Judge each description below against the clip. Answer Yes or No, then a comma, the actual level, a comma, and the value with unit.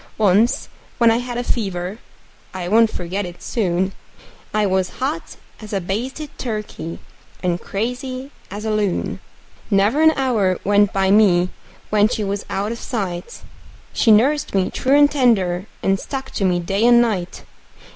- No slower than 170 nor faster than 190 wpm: No, average, 160 wpm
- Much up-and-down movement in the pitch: No, average, 4.2 semitones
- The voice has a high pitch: Yes, high, 210 Hz